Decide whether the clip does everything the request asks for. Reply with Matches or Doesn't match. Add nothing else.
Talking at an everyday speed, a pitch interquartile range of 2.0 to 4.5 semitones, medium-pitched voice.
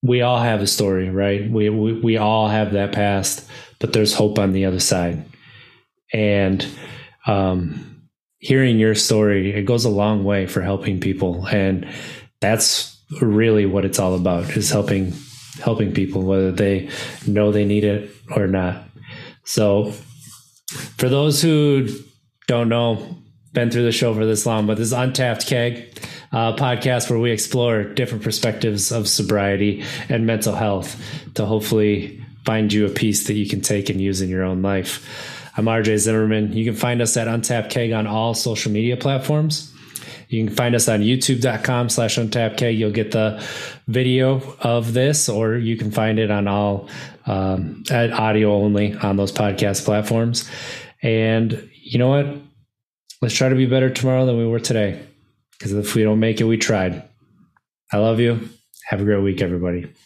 Doesn't match